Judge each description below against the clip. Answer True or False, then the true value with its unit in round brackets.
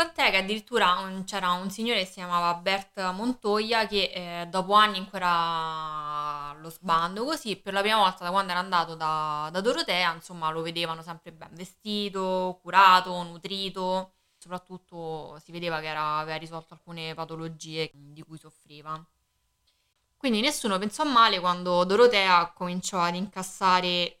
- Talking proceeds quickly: False (145 wpm)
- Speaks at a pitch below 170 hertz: False (180 Hz)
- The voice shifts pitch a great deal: False (2.9 semitones)